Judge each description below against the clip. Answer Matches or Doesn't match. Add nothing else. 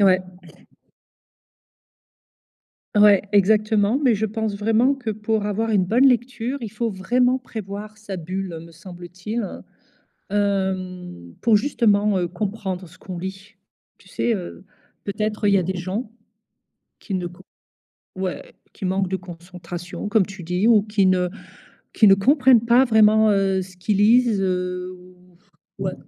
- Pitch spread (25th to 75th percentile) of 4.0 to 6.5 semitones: Doesn't match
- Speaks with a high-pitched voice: Matches